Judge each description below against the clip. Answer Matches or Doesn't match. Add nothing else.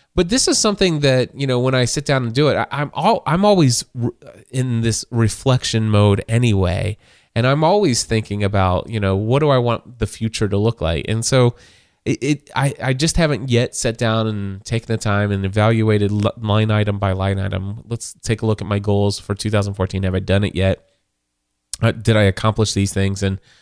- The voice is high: Doesn't match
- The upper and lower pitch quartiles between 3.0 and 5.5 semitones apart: Matches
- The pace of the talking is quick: Matches